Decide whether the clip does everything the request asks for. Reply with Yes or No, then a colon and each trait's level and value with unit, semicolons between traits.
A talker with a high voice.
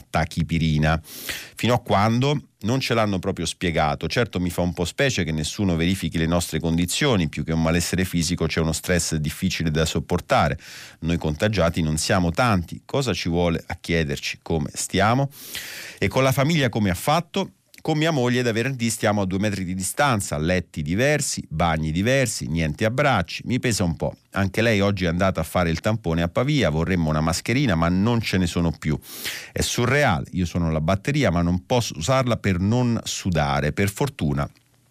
No: very low, 90 Hz